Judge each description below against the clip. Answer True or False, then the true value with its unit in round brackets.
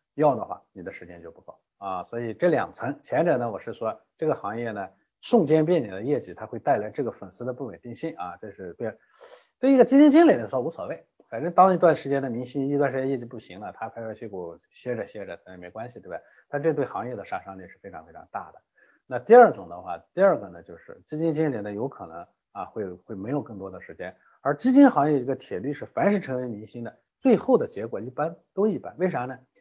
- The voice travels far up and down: True (6.1 semitones)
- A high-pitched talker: False (135 Hz)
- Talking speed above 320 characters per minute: True (355 characters per minute)